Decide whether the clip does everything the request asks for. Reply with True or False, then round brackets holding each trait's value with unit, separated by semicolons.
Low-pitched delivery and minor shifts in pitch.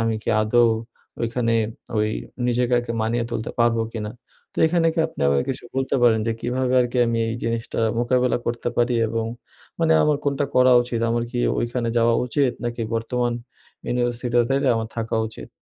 True (120 Hz; 1.5 semitones)